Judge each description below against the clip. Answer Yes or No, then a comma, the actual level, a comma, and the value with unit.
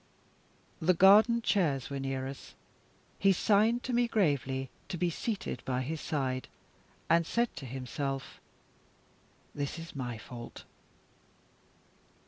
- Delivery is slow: Yes, slow, 120 wpm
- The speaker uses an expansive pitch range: Yes, wide, 6.8 semitones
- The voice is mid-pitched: Yes, medium, 150 Hz